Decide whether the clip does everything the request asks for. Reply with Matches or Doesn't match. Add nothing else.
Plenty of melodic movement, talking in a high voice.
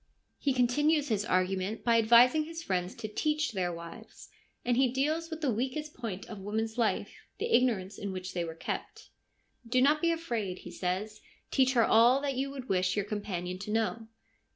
Matches